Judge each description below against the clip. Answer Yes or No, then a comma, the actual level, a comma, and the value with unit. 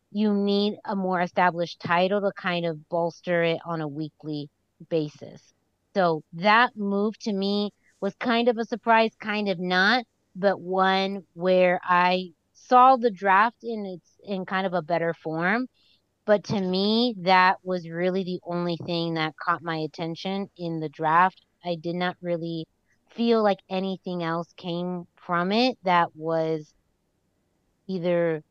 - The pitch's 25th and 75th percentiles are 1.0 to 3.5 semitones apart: Yes, average, 3.0 semitones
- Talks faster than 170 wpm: No, average, 155 wpm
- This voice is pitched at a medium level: Yes, medium, 180 Hz